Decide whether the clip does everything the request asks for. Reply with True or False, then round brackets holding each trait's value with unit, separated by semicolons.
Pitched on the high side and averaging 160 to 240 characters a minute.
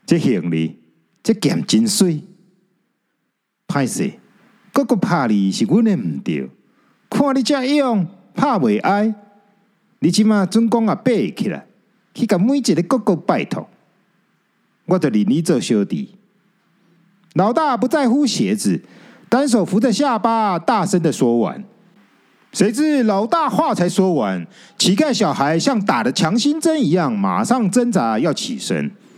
True (210 Hz; 195 characters per minute)